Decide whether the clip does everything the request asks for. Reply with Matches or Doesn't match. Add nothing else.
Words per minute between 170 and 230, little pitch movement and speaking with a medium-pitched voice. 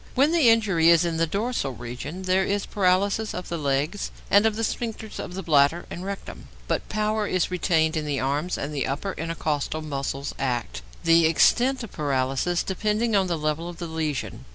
Doesn't match